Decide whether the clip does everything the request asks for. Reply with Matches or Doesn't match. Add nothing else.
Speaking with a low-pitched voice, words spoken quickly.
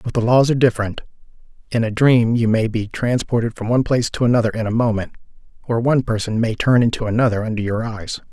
Matches